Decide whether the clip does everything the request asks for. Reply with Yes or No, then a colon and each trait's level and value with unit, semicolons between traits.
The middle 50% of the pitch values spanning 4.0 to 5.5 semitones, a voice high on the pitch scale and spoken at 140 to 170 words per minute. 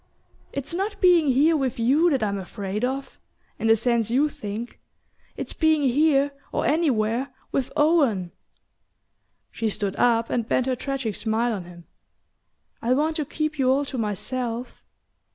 Yes: average, 4.6 semitones; very high, 255 Hz; average, 155 wpm